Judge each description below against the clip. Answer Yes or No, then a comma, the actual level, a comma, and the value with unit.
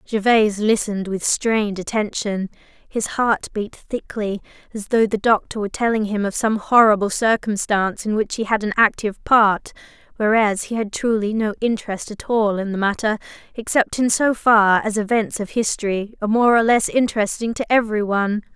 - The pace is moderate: Yes, average, 170 wpm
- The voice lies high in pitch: Yes, high, 215 Hz